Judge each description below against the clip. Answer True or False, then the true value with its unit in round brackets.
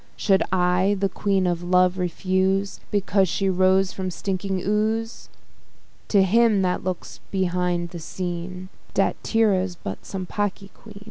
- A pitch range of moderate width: False (1.7 semitones)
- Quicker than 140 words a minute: False (135 wpm)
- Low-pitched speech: False (190 Hz)